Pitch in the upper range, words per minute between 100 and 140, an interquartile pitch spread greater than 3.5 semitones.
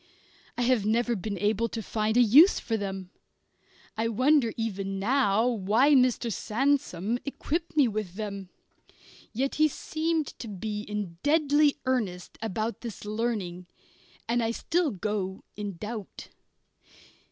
Yes: high, 225 Hz; slow, 135 wpm; average, 4.1 semitones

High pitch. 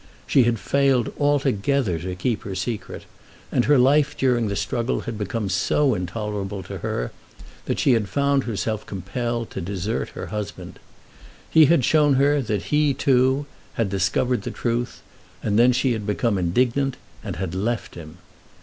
No: low, 115 Hz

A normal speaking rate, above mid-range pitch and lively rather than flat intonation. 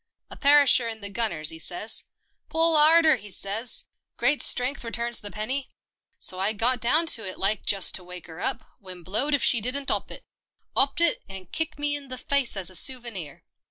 No: fast, 210 wpm; high, 235 Hz; wide, 6.3 semitones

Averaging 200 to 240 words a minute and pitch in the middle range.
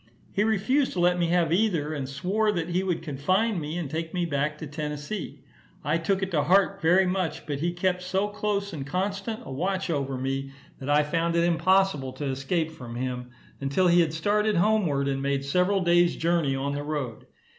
Yes: fast, 205 wpm; medium, 170 Hz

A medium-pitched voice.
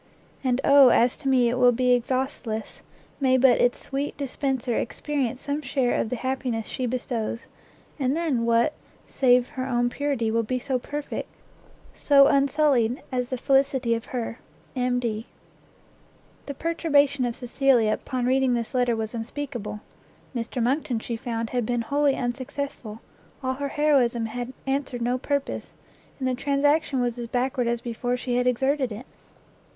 No: very high, 250 Hz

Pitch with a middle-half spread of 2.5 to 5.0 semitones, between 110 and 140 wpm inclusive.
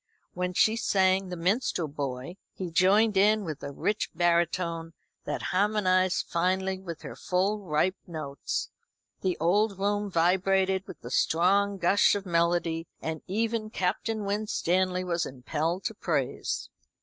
Yes: average, 3.0 semitones; slow, 135 wpm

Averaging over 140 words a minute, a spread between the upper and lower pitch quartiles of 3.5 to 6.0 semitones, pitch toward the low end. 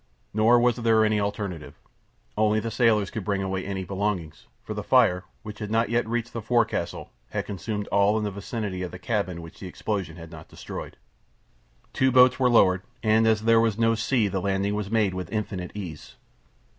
No: average, 195 wpm; average, 3.0 semitones; low, 105 Hz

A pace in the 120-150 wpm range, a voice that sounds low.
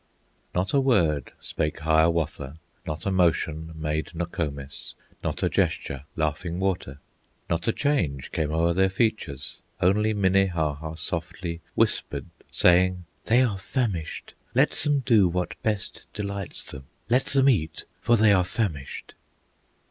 Yes: slow, 135 wpm; very low, 90 Hz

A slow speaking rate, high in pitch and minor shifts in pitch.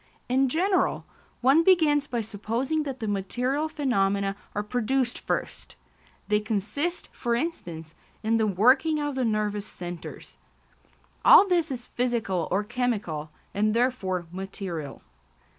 No: slow, 125 wpm; high, 235 Hz; average, 5.3 semitones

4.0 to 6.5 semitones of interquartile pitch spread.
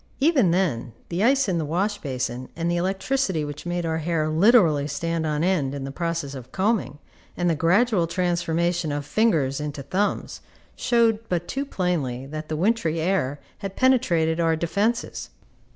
Yes: average, 4.5 semitones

